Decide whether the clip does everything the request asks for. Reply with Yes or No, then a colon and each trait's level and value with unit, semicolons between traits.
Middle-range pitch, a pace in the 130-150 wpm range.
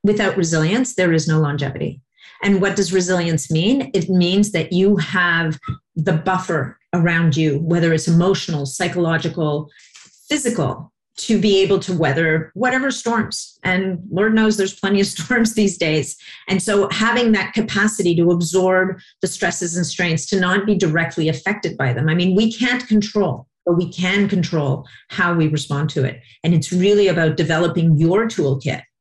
No: medium, 180 Hz; average, 165 wpm